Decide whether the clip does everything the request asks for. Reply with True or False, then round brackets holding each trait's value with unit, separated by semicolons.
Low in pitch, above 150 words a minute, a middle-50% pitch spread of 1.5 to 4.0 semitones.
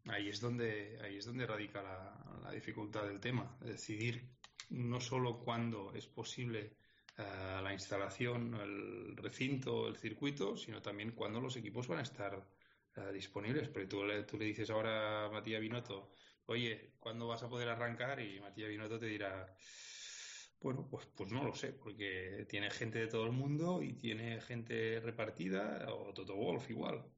True (110 Hz; 170 wpm; 2.7 semitones)